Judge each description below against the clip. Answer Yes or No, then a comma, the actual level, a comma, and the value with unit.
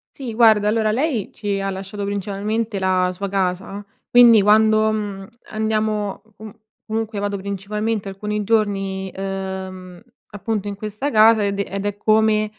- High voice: Yes, high, 205 Hz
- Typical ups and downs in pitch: No, narrow, 1.9 semitones